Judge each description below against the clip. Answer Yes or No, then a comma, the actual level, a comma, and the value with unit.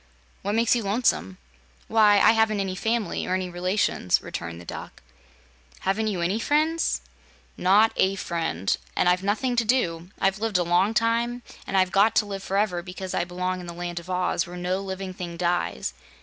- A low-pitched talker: No, high, 190 Hz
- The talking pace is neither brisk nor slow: Yes, average, 190 wpm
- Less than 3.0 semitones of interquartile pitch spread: No, average, 3.5 semitones